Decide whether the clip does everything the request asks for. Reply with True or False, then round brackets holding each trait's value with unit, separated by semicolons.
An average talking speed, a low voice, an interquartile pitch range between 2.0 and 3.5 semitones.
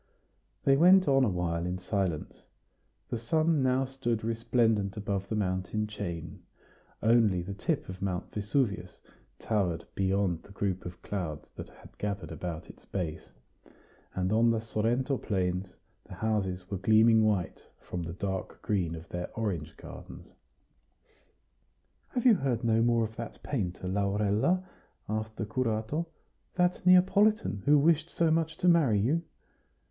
False (145 wpm; 105 Hz; 5.5 semitones)